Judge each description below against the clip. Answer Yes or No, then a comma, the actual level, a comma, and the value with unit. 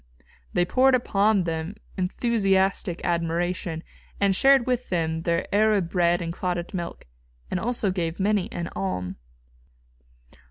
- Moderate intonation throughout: Yes, average, 3.4 semitones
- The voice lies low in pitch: No, medium, 180 Hz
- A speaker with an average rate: No, slow, 125 wpm